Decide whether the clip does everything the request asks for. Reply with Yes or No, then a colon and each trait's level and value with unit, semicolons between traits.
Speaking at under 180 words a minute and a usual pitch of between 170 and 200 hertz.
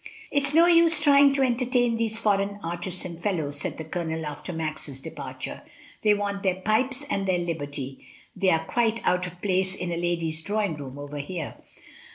No: average, 195 wpm; medium, 185 Hz